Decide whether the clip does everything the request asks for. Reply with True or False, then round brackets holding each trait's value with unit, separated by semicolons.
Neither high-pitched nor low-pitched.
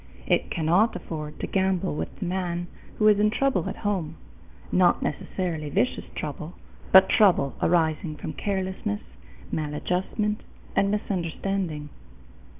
True (180 Hz)